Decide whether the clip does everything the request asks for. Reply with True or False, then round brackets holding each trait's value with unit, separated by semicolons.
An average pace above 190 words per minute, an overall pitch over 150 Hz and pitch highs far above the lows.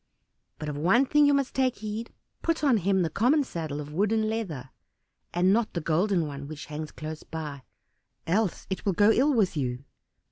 True (200 wpm; 190 Hz; 6.6 semitones)